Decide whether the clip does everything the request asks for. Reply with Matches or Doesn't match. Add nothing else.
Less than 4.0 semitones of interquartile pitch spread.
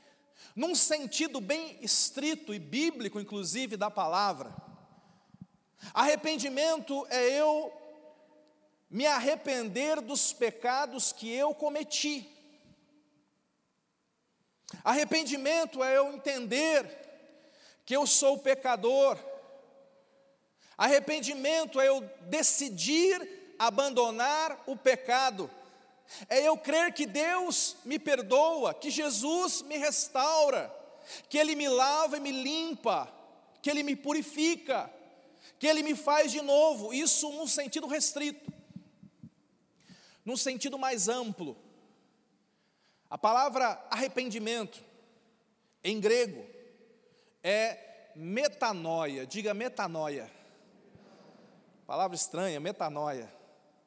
Doesn't match